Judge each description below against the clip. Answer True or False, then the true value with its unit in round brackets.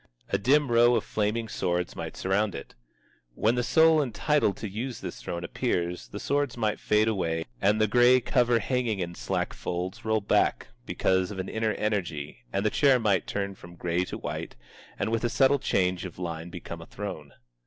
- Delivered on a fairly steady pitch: False (4.9 semitones)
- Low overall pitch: True (105 Hz)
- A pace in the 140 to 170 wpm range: False (195 wpm)